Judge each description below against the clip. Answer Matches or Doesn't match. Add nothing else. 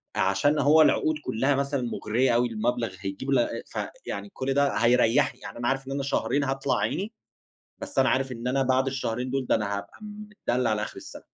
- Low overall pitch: Matches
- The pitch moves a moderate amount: Matches